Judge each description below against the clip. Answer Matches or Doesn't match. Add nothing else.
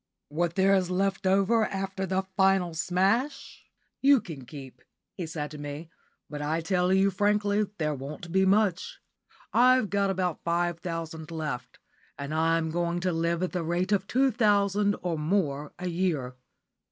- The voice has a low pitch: Doesn't match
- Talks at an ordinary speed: Matches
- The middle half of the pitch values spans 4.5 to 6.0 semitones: Doesn't match